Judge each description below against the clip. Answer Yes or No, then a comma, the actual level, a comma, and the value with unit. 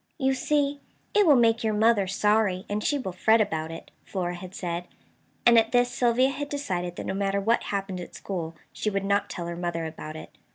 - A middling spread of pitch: Yes, average, 5.0 semitones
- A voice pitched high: Yes, high, 200 Hz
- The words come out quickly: Yes, fast, 215 wpm